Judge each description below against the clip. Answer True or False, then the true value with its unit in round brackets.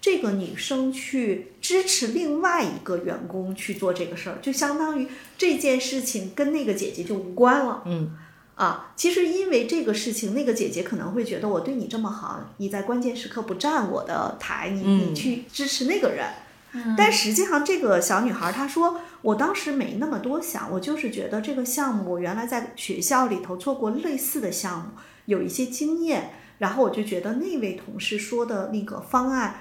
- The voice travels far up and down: True (6.1 semitones)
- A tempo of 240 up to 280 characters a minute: False (290 characters per minute)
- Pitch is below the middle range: False (245 Hz)